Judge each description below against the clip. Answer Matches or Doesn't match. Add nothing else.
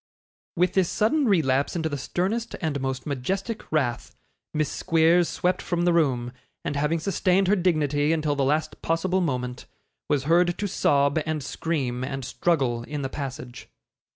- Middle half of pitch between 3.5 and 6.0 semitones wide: Matches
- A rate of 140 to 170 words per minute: Matches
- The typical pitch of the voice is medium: Matches